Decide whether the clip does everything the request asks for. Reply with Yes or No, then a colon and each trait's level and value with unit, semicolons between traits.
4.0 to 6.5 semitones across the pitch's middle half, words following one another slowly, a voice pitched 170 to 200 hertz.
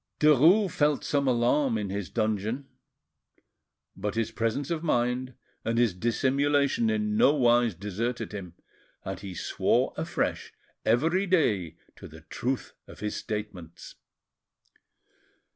No: wide, 5.6 semitones; slow, 125 wpm; low, 120 Hz